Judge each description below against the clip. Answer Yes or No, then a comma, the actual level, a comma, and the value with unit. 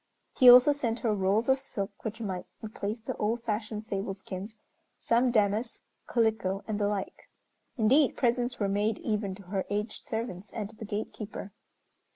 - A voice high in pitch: Yes, high, 215 Hz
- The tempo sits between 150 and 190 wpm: Yes, average, 170 wpm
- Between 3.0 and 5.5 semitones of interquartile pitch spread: No, narrow, 2.5 semitones